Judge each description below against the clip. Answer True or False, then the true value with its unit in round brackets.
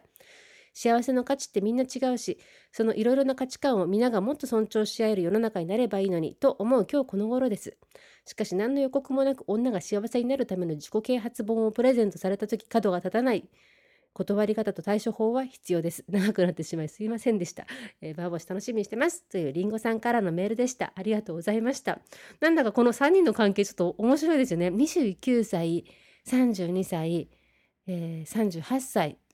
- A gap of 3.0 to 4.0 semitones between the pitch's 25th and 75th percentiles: False (5.2 semitones)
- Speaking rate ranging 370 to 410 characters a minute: True (400 characters per minute)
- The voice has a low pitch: False (225 Hz)